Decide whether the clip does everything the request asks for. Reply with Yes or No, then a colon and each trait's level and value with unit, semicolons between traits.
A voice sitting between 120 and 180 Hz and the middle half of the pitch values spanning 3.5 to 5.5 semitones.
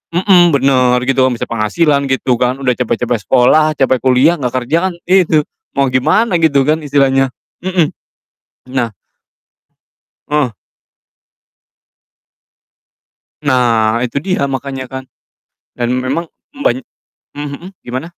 Yes: low, 135 Hz; average, 3.8 semitones